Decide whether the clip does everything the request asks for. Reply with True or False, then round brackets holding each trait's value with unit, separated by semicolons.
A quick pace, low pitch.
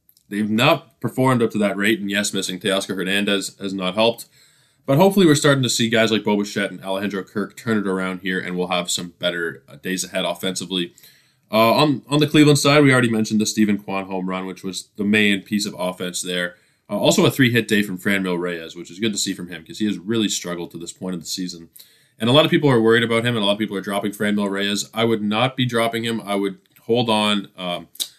True (250 wpm; 105 Hz)